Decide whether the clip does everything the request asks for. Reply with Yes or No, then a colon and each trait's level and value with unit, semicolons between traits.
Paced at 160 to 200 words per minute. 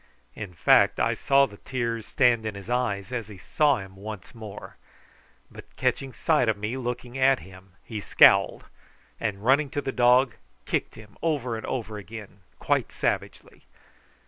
Yes: average, 165 wpm